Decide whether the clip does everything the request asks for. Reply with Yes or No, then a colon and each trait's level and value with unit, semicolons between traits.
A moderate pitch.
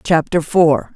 Yes: medium, 160 Hz